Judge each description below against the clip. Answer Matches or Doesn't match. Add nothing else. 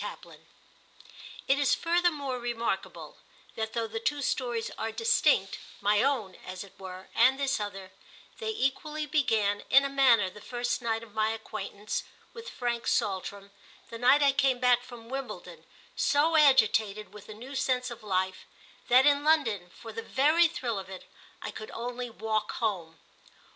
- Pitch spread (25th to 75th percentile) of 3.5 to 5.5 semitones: Matches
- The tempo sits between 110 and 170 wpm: Matches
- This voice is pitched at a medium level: Doesn't match